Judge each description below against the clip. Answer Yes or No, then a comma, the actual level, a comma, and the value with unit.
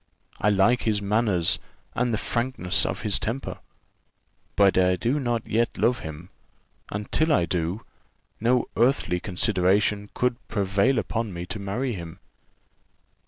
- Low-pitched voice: Yes, low, 105 Hz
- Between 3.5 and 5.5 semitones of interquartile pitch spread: Yes, average, 4.3 semitones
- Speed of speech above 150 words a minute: No, average, 140 wpm